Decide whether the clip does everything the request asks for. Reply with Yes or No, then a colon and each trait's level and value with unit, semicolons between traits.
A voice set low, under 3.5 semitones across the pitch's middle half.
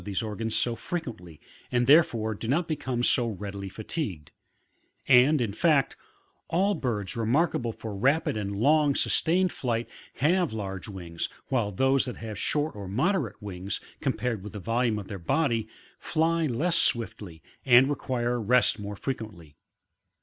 No: low, 115 Hz; average, 5.3 semitones